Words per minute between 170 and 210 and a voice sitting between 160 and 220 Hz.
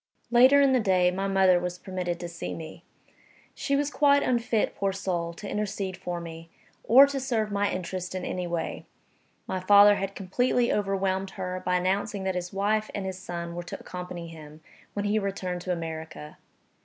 Yes: average, 185 wpm; high, 190 Hz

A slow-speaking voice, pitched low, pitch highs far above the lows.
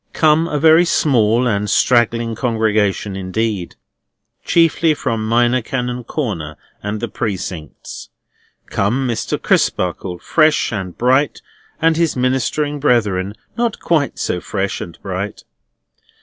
Yes: slow, 120 wpm; low, 115 Hz; wide, 6.0 semitones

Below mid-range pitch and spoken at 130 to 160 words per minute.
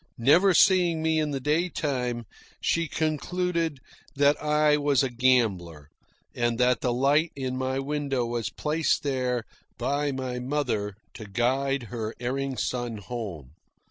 Yes: low, 130 Hz; average, 140 wpm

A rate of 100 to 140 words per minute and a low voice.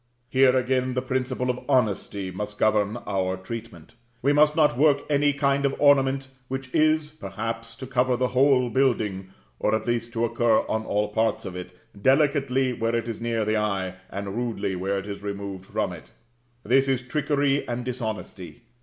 No: average, 180 wpm; low, 120 Hz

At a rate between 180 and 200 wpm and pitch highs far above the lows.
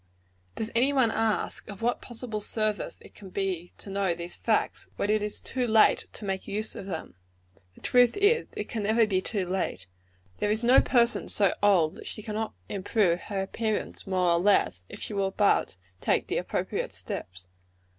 No: average, 190 wpm; average, 2.8 semitones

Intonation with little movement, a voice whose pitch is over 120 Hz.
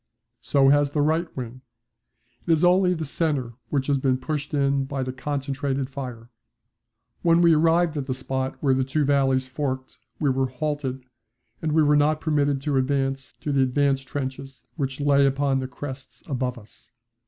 Yes: narrow, 2.0 semitones; medium, 140 Hz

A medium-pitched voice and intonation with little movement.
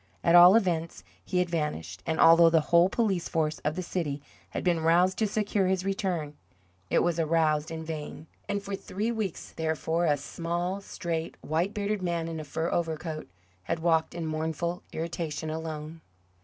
Yes: medium, 165 Hz; narrow, 2.2 semitones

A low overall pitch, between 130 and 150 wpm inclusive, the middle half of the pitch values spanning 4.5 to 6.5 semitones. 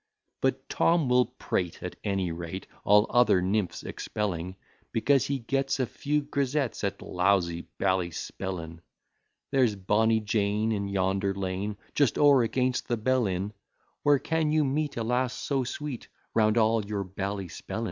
Yes: low, 110 Hz; average, 145 wpm; average, 5.1 semitones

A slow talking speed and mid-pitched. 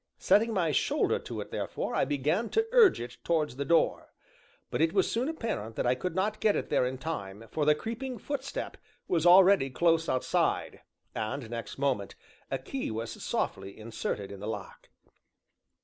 No: average, 180 wpm; medium, 155 Hz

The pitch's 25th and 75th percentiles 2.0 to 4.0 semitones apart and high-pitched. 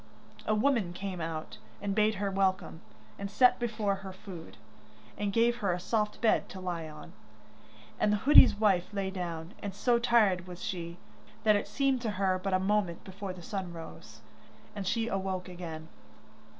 Yes: average, 2.8 semitones; high, 195 Hz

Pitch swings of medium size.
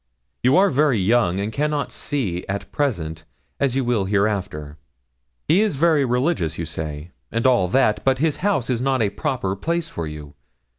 No: wide, 7.2 semitones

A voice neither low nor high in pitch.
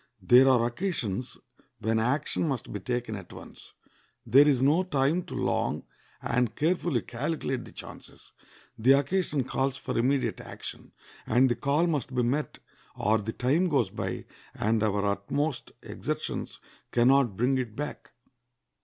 No: low, 130 Hz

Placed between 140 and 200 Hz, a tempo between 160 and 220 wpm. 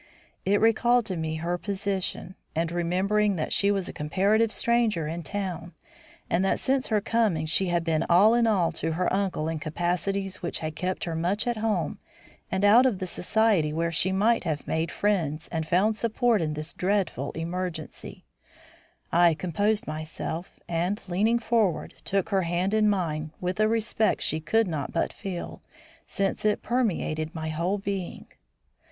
Yes: medium, 185 Hz; average, 170 wpm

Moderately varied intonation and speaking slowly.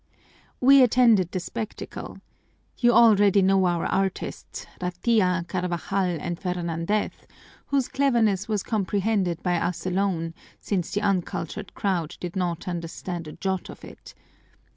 Yes: average, 3.2 semitones; slow, 125 wpm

